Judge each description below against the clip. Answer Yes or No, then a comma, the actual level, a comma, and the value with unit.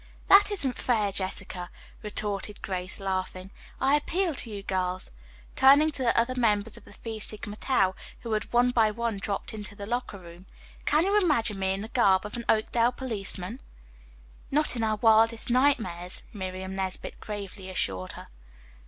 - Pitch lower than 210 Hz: No, high, 215 Hz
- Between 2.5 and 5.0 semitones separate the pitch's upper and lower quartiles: Yes, average, 4.1 semitones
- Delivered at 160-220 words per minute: Yes, average, 170 wpm